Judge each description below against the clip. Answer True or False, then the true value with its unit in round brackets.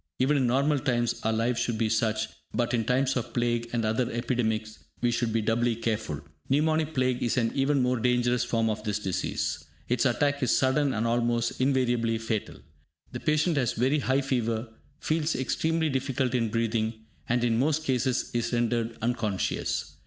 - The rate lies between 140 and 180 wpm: True (175 wpm)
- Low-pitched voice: True (120 Hz)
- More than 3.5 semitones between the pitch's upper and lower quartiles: False (2.5 semitones)